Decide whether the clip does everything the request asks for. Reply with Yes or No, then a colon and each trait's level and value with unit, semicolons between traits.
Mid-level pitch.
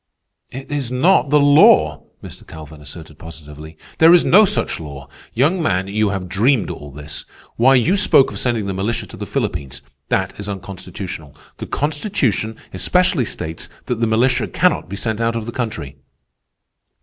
No: low, 110 Hz